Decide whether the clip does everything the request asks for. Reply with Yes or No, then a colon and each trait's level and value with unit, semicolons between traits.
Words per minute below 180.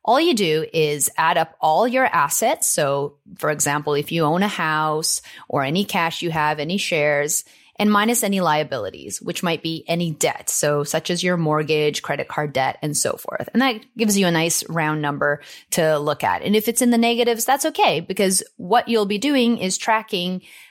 No: fast, 205 wpm